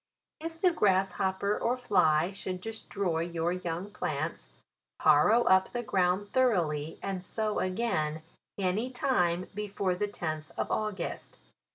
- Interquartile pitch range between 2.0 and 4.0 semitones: Yes, average, 3.5 semitones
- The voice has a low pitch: No, high, 190 Hz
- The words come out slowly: Yes, slow, 130 wpm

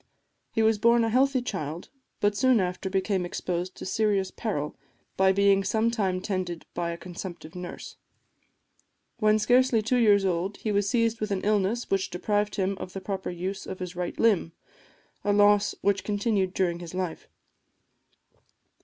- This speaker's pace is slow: No, average, 165 wpm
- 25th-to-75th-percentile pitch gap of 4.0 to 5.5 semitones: No, average, 2.7 semitones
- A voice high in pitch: Yes, high, 195 Hz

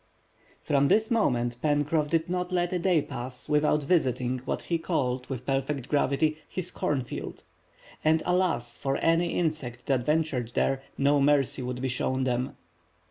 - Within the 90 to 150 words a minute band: No, average, 160 wpm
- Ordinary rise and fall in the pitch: Yes, average, 4.1 semitones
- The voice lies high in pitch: No, medium, 140 Hz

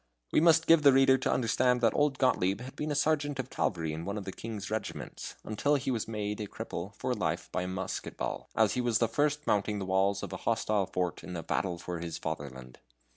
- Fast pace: Yes, fast, 235 wpm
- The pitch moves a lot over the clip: Yes, wide, 5.9 semitones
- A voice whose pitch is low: Yes, low, 110 Hz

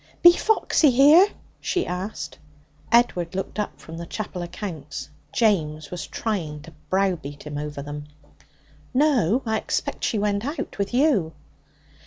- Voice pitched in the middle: No, high, 195 Hz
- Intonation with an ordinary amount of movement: No, wide, 7.1 semitones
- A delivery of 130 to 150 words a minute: Yes, average, 140 wpm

